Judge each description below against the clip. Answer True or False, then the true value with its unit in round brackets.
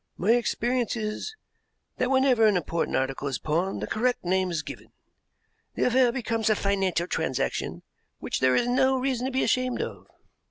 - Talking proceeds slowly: False (170 wpm)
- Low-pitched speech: False (225 Hz)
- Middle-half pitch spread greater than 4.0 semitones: True (5.6 semitones)